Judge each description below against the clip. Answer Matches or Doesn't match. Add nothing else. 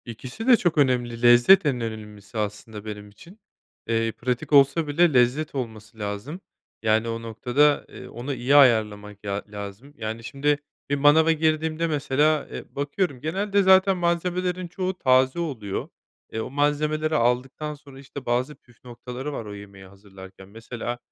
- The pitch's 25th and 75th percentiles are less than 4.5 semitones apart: Doesn't match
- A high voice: Doesn't match